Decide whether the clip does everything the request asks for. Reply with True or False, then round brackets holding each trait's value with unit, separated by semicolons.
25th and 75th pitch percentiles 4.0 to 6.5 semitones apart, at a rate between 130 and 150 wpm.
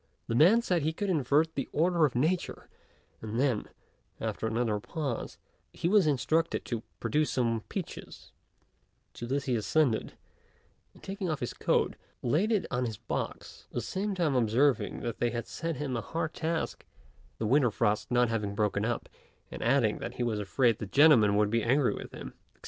False (5.6 semitones; 185 wpm)